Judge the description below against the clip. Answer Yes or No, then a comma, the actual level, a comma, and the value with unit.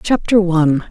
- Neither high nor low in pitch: Yes, medium, 180 Hz